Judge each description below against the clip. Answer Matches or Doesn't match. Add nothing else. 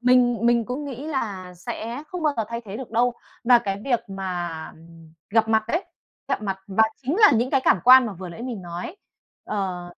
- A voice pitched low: Doesn't match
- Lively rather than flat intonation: Doesn't match